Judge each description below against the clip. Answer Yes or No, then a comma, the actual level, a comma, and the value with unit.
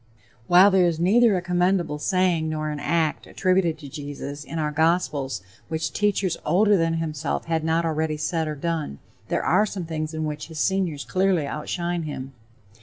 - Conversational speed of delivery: Yes, average, 180 wpm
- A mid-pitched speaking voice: Yes, medium, 160 Hz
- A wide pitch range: No, average, 2.8 semitones